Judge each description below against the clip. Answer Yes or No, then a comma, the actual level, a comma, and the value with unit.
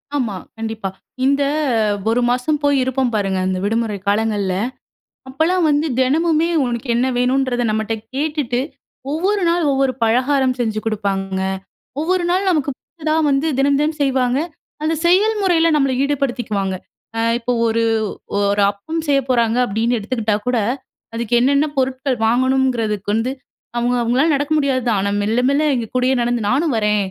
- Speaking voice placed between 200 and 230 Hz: No, very high, 255 Hz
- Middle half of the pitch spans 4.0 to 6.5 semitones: Yes, average, 4.3 semitones